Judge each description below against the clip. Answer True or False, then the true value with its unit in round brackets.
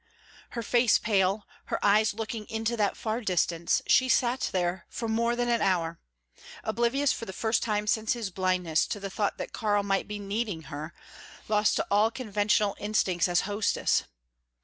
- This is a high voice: True (210 Hz)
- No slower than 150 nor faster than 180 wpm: True (170 wpm)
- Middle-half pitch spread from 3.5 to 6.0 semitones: False (3.1 semitones)